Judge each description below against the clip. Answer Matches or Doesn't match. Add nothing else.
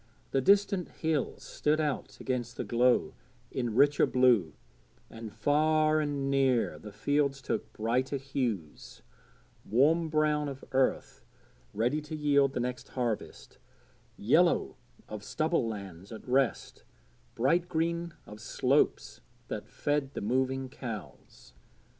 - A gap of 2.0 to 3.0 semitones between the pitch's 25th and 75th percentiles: Doesn't match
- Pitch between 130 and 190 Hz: Matches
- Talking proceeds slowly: Matches